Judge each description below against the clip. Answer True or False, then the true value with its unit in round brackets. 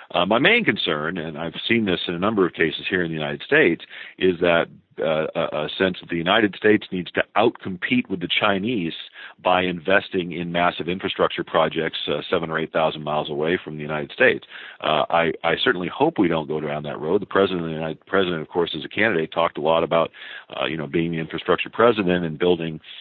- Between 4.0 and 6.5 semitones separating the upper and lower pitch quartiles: False (2.6 semitones)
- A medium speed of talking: False (225 wpm)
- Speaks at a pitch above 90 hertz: False (85 Hz)